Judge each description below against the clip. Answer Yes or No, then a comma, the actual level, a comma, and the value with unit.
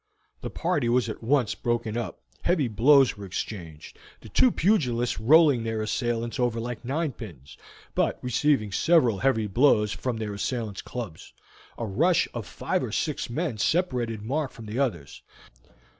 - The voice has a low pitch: Yes, low, 120 Hz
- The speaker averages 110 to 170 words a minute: Yes, average, 155 wpm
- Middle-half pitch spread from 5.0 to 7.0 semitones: No, average, 4.2 semitones